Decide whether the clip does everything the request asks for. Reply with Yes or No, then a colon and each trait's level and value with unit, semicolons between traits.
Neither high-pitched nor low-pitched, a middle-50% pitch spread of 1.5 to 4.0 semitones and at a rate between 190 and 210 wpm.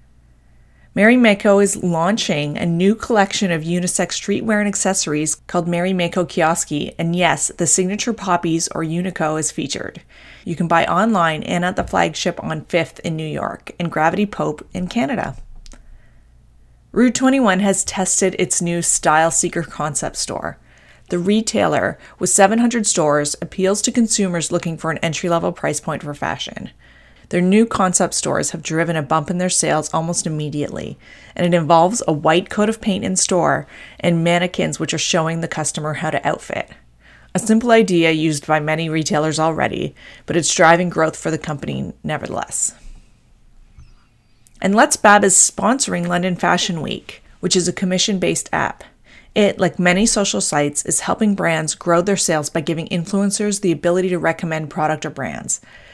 No: medium, 175 Hz; average, 3.5 semitones; average, 165 wpm